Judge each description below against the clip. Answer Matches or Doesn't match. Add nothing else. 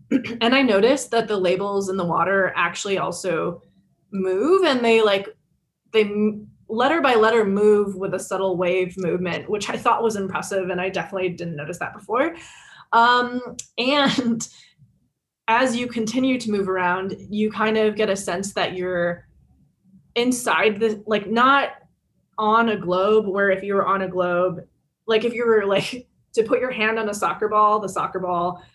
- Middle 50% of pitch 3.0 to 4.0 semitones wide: Matches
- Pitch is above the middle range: Matches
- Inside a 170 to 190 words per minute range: Matches